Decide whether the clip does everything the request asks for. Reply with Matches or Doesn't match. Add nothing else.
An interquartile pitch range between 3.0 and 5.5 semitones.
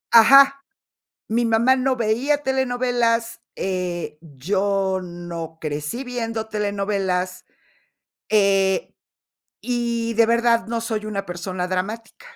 Matches